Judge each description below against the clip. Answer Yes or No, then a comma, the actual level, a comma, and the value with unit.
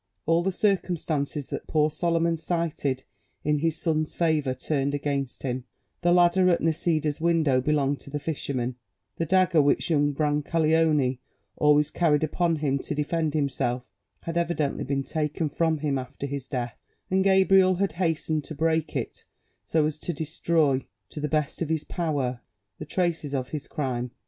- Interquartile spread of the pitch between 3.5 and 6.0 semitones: No, average, 2.9 semitones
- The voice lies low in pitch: No, medium, 155 Hz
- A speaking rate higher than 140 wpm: Yes, average, 165 wpm